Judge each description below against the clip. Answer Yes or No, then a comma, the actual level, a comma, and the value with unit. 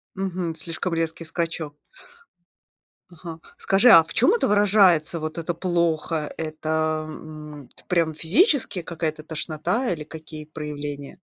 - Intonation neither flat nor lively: No, narrow, 2.1 semitones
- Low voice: No, medium, 160 Hz